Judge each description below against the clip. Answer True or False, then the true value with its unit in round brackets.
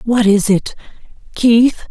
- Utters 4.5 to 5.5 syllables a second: False (3.8 syllables/s)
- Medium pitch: False (225 Hz)